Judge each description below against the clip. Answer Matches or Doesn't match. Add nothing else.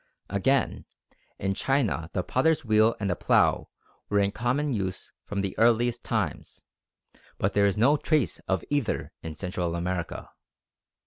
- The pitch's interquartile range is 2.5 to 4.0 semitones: Doesn't match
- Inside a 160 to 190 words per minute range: Doesn't match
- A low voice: Matches